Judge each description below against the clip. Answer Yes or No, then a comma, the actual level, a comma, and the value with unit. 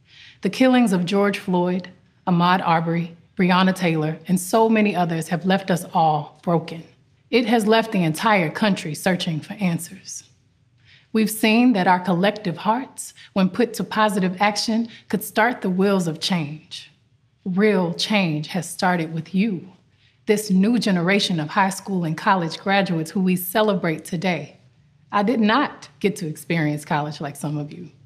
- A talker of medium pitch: Yes, medium, 180 Hz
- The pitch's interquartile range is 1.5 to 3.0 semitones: No, average, 4.3 semitones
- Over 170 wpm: No, average, 160 wpm